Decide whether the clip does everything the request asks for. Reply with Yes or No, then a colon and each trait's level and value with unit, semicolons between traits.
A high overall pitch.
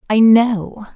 Yes: high, 220 Hz